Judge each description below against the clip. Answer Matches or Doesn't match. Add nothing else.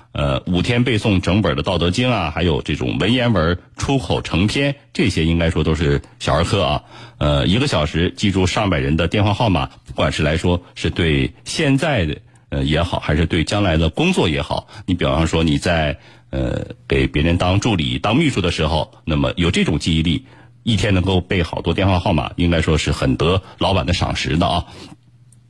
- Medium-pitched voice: Doesn't match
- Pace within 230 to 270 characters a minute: Doesn't match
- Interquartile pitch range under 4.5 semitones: Doesn't match